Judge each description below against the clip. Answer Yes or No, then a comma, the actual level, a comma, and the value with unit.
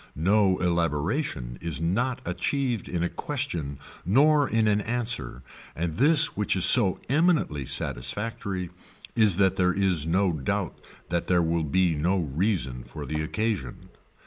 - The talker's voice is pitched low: Yes, very low, 90 Hz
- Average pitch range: No, wide, 5.9 semitones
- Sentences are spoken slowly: No, average, 145 wpm